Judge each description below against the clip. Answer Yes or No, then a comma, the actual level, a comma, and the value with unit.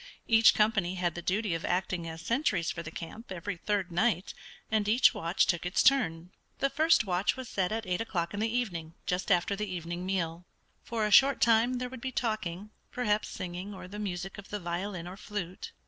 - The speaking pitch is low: No, high, 195 Hz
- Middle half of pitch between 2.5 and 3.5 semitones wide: No, average, 4.0 semitones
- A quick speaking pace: Yes, fast, 210 wpm